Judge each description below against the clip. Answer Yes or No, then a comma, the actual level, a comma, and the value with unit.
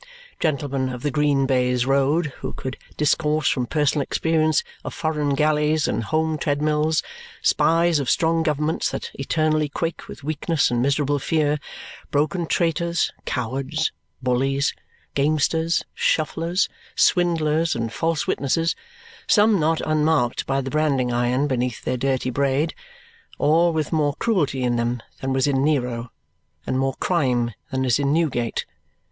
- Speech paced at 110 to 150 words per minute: Yes, average, 140 wpm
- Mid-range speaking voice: Yes, medium, 145 Hz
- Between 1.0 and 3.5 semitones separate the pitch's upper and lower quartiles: Yes, average, 3.1 semitones